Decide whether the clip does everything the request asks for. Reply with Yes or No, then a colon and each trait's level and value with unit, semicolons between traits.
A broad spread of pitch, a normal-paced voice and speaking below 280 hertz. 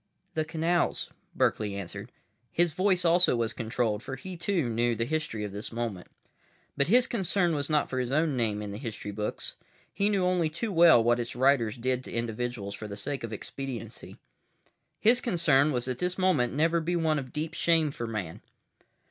Yes: wide, 6.6 semitones; average, 190 wpm; low, 135 Hz